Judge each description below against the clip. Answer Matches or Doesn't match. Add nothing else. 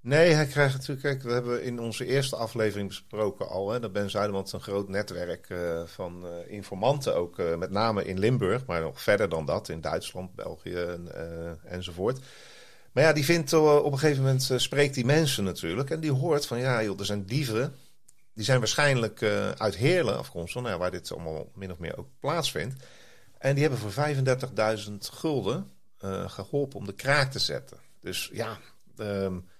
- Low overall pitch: Matches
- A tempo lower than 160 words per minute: Doesn't match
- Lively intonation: Matches